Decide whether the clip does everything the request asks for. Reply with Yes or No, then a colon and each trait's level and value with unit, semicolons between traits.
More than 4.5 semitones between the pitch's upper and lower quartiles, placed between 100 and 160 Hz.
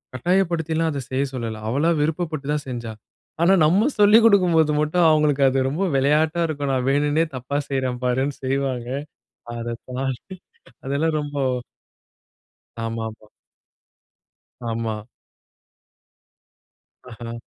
No: average, 4.2 semitones; medium, 140 Hz